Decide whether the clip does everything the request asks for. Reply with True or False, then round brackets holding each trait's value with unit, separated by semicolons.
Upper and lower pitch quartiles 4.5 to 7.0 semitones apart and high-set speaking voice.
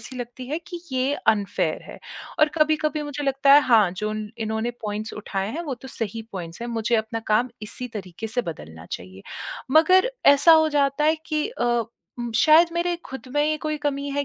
True (5.6 semitones; 250 Hz)